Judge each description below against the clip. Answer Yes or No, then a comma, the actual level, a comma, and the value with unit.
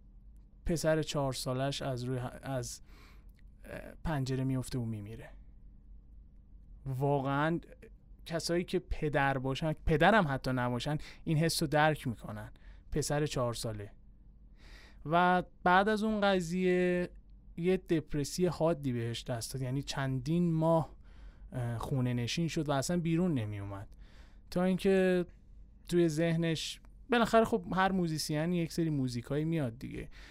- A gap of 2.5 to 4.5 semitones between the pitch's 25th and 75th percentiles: No, wide, 5.6 semitones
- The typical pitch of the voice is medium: Yes, medium, 145 Hz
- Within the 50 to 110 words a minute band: No, average, 125 wpm